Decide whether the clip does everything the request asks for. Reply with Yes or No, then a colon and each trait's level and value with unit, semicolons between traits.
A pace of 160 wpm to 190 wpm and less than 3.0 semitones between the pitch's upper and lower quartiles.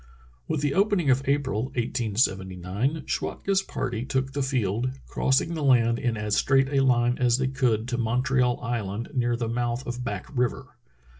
Yes: average, 165 wpm; narrow, 2.6 semitones